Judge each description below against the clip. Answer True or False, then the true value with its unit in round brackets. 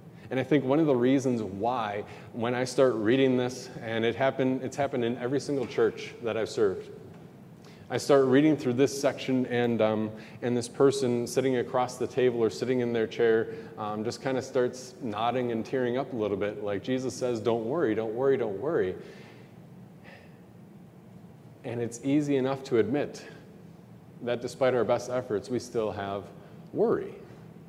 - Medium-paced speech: True (175 wpm)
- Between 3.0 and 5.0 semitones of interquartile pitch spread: False (2.6 semitones)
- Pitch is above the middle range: False (125 Hz)